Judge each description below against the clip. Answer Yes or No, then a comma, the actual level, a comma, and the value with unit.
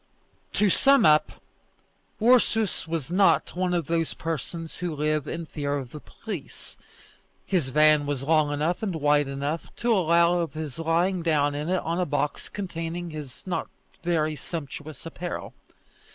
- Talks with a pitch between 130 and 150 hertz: No, medium, 165 Hz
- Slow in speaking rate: No, average, 155 wpm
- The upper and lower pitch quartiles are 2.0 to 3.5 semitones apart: Yes, average, 2.9 semitones